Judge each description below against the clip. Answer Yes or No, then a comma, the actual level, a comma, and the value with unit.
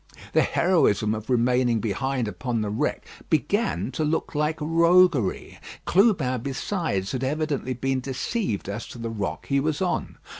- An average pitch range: No, wide, 5.7 semitones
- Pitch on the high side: No, low, 130 Hz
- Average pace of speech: Yes, average, 150 wpm